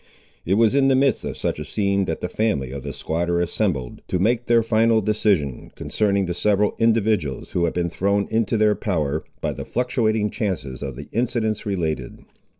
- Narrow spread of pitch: No, average, 4.8 semitones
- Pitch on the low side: Yes, low, 100 Hz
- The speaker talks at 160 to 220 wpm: Yes, average, 190 wpm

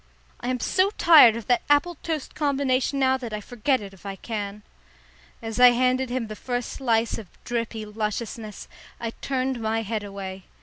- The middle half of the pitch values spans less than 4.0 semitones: Yes, average, 3.4 semitones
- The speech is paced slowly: No, average, 180 wpm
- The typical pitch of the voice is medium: No, high, 235 Hz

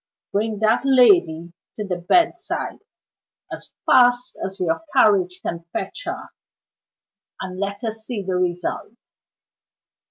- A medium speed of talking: No, slow, 120 wpm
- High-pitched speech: Yes, high, 205 Hz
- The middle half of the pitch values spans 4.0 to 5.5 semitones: Yes, average, 5.2 semitones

